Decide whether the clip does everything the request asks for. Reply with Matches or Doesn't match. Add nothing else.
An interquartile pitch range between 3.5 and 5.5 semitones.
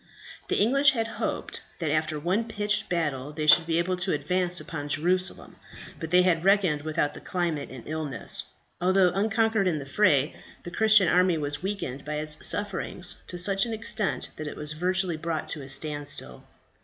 Matches